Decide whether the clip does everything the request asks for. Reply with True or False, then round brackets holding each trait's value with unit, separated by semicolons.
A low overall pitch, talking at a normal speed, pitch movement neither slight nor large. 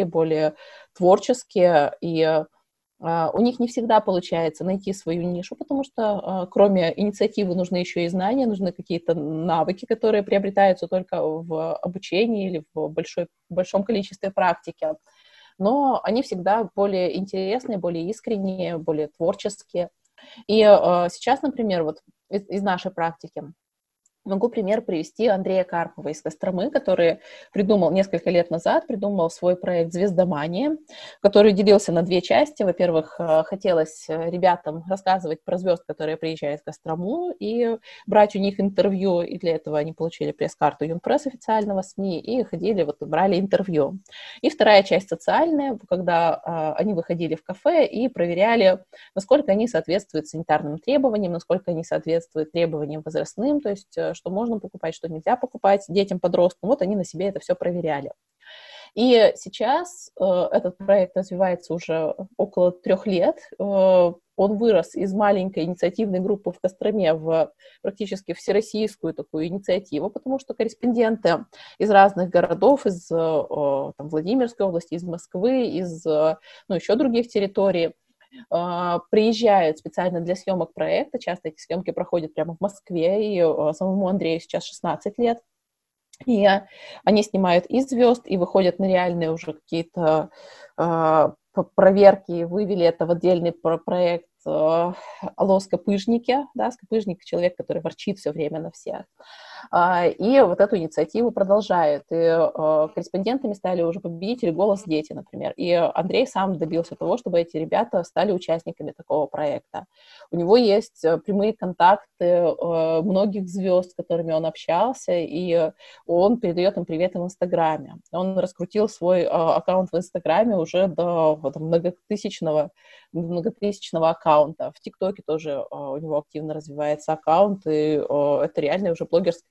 False (185 Hz; 135 wpm; 3.9 semitones)